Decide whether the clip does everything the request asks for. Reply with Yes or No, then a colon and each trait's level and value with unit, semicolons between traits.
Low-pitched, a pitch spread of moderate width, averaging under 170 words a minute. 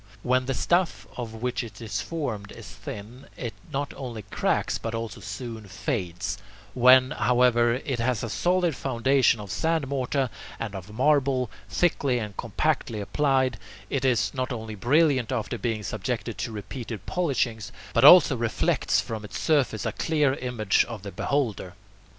Yes: low, 125 Hz; average, 3.8 semitones; average, 155 wpm